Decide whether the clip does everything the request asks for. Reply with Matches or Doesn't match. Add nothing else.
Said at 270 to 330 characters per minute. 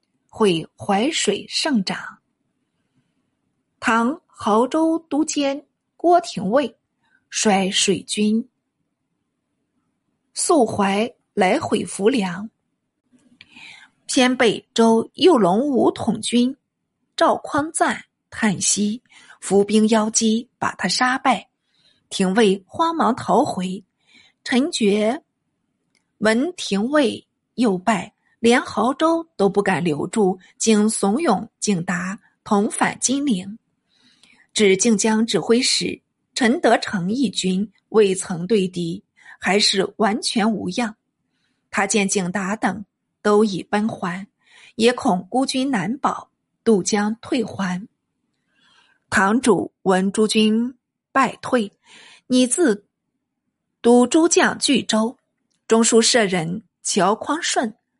Doesn't match